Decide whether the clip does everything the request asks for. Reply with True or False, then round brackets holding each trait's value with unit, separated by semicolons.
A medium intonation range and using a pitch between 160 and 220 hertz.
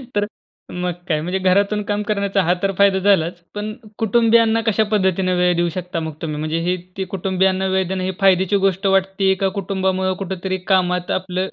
False (1.7 semitones; 190 Hz)